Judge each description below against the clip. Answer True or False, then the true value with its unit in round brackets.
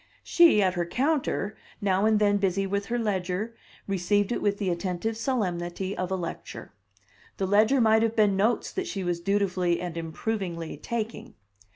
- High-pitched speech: True (200 Hz)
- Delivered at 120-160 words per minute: False (170 wpm)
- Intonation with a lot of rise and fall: False (3.4 semitones)